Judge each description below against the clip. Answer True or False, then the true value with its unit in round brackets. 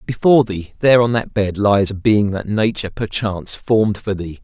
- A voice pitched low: True (105 Hz)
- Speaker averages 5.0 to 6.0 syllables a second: True (5.5 syllables/s)